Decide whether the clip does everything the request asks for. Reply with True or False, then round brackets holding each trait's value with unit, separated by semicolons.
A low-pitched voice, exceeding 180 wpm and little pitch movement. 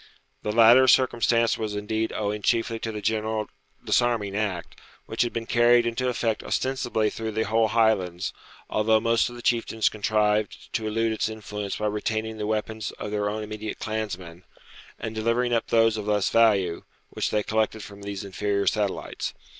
False (110 Hz; 170 wpm; 1.5 semitones)